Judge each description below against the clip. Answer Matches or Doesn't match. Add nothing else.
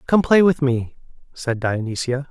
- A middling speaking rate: Matches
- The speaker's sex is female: Doesn't match